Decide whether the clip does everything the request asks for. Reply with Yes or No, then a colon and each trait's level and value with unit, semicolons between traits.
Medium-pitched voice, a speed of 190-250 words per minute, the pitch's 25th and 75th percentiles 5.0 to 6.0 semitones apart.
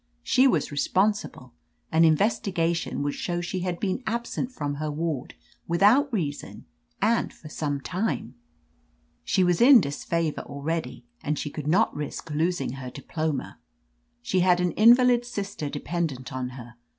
No: medium, 170 Hz; average, 155 wpm; wide, 5.5 semitones